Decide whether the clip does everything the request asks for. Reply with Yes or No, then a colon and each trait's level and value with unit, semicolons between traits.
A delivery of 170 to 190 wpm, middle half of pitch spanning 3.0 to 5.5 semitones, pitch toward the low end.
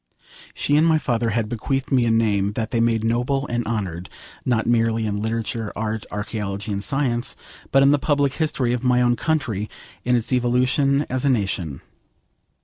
Yes: average, 180 wpm; average, 3.3 semitones; low, 120 Hz